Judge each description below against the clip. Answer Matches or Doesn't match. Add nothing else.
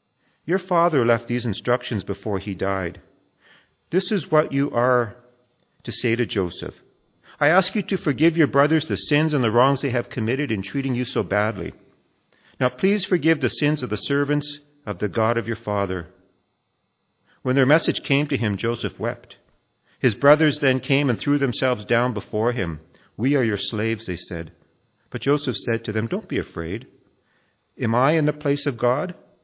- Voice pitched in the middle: Doesn't match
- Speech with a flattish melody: Doesn't match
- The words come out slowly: Doesn't match